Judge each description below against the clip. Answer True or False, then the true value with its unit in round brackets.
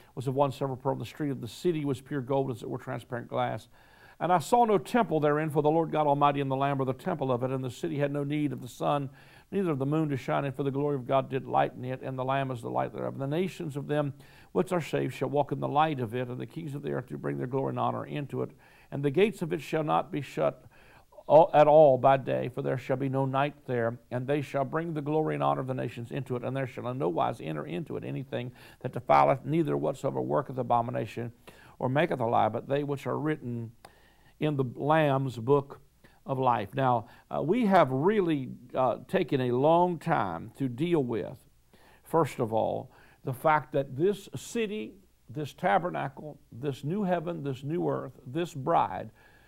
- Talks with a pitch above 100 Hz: True (140 Hz)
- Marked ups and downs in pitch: False (3.4 semitones)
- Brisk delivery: True (235 wpm)